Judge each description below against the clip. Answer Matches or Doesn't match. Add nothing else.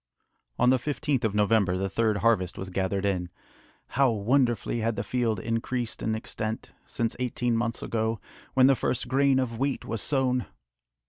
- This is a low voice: Matches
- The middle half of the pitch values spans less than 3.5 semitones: Matches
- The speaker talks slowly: Doesn't match